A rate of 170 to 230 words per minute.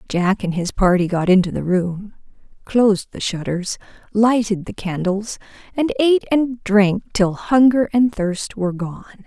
No: average, 155 wpm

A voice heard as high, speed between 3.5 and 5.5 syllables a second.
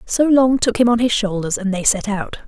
Yes: high, 220 Hz; 5.2 syllables/s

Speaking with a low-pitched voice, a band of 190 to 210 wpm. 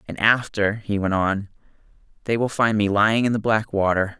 Yes: low, 105 Hz; average, 200 wpm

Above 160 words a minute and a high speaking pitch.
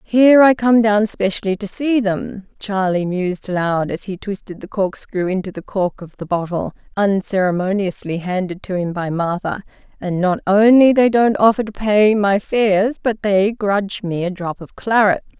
Yes: average, 180 wpm; high, 200 Hz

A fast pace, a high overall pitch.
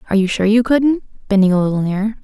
Yes: fast, 240 wpm; high, 210 Hz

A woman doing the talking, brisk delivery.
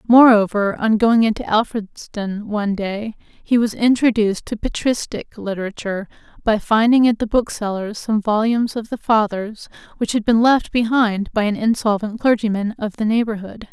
No: female; average, 155 wpm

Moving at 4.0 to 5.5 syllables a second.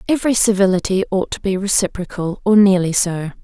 No: 5.8 syllables/s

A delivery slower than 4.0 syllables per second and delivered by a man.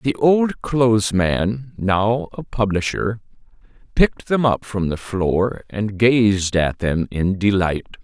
Yes: 3.5 syllables/s; male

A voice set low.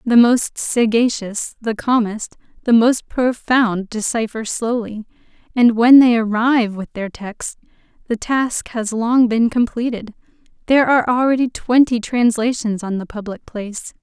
No: high, 230 Hz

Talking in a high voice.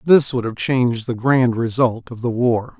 No: low, 120 Hz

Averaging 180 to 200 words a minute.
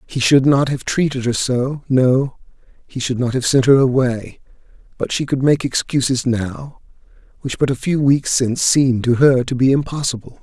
Yes: average, 190 wpm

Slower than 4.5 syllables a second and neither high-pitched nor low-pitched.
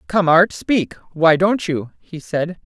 Yes: 3.6 syllables/s; medium, 175 Hz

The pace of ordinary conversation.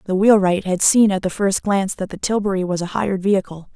No: fast, 240 wpm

